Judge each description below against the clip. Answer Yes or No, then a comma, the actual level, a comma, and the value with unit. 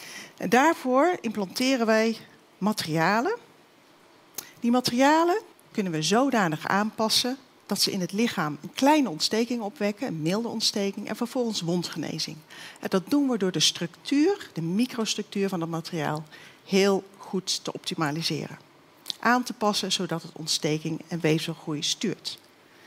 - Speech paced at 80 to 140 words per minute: Yes, slow, 135 wpm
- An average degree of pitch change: No, wide, 6.5 semitones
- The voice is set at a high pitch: Yes, high, 200 Hz